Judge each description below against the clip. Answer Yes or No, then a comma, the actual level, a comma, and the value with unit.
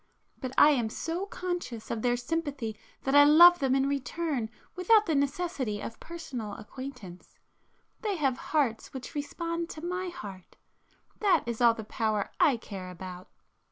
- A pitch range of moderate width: No, wide, 6.8 semitones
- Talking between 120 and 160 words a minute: Yes, average, 155 wpm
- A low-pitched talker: No, very high, 275 Hz